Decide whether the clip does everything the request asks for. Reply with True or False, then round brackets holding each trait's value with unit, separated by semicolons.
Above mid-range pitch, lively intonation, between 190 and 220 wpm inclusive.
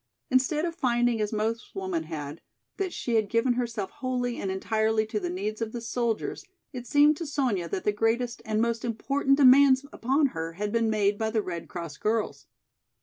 False (225 Hz; 3.4 semitones; 195 wpm)